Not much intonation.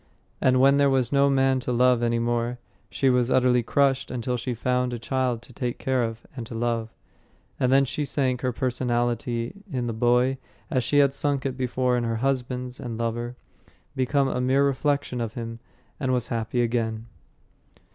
Yes: narrow, 1.9 semitones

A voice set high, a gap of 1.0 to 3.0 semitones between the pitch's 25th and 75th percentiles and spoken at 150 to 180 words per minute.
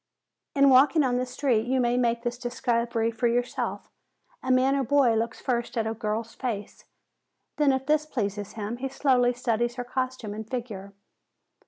Yes: high, 245 Hz; narrow, 2.4 semitones; average, 175 wpm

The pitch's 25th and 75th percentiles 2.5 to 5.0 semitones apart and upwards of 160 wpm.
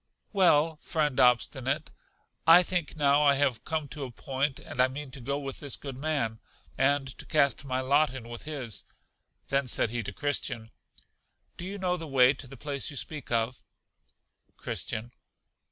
Yes: average, 2.9 semitones; average, 175 wpm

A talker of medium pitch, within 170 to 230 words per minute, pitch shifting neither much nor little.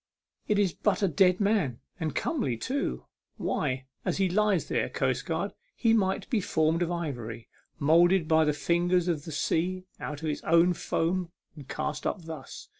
Yes: medium, 170 Hz; average, 175 wpm; average, 3.6 semitones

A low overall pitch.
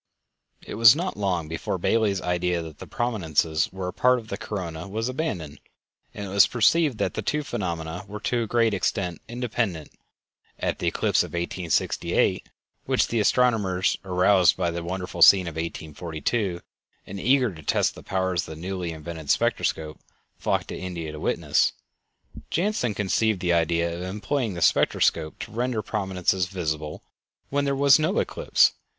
Yes: very low, 95 Hz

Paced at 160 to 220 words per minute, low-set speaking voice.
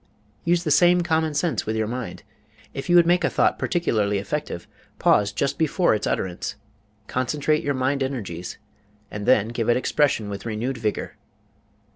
Yes: average, 165 wpm; low, 130 Hz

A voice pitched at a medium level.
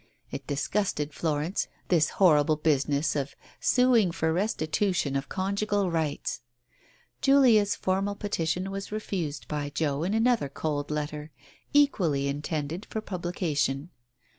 Yes: medium, 165 Hz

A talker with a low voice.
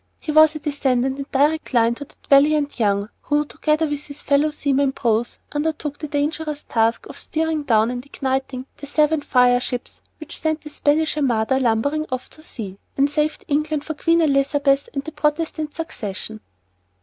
No: very high, 285 Hz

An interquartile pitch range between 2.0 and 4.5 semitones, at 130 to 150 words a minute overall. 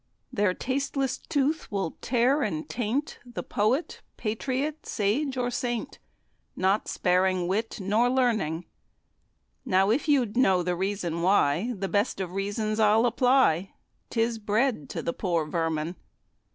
No: average, 5.2 semitones; slow, 135 wpm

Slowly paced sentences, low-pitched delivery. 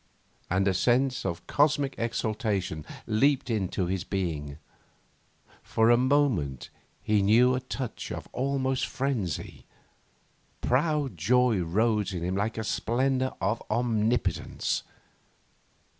Yes: slow, 115 wpm; low, 115 Hz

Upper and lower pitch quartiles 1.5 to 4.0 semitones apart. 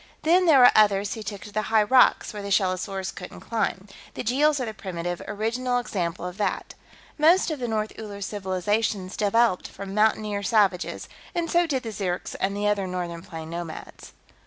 Yes: average, 3.6 semitones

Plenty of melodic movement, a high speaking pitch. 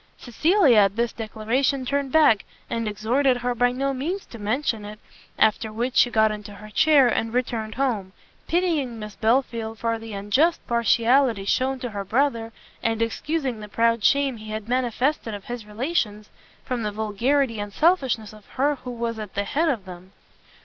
No: average, 3.9 semitones; high, 230 Hz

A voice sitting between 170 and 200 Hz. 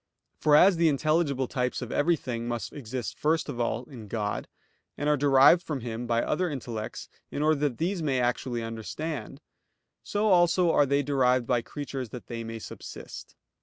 No: low, 135 Hz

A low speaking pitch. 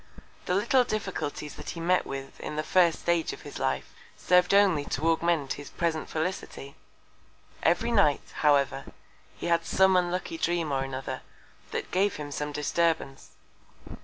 No: medium, 170 Hz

